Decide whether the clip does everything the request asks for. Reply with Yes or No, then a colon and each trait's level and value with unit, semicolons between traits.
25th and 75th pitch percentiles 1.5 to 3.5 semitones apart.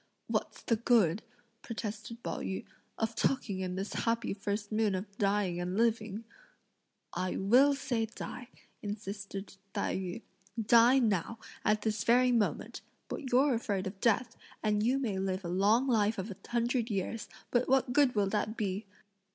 Yes: average, 3.1 semitones